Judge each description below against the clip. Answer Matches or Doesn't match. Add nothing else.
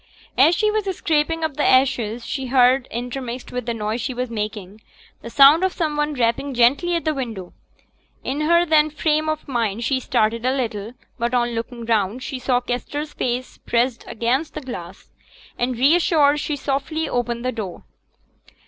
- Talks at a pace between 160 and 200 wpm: Matches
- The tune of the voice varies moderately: Matches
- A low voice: Doesn't match